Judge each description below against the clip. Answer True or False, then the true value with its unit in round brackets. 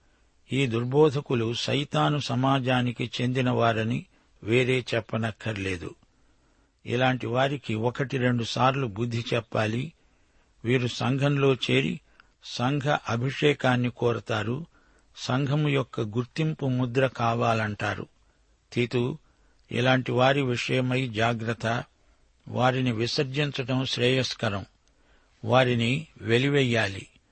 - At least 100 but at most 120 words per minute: False (75 wpm)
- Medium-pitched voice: False (125 Hz)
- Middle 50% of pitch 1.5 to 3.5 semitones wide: True (2.5 semitones)